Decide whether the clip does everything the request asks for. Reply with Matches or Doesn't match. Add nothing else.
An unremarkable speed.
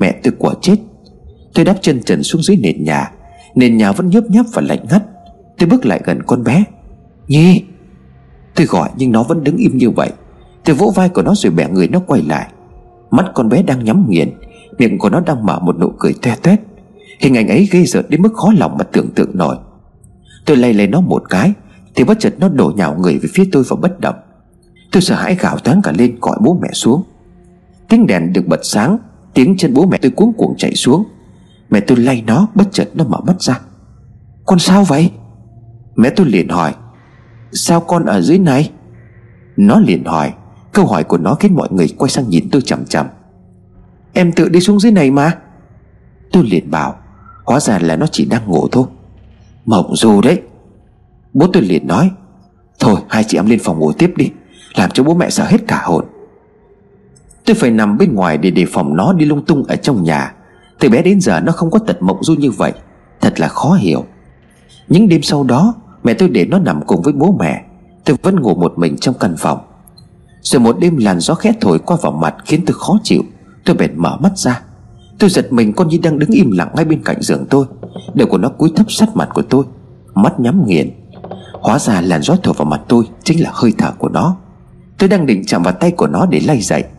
Matches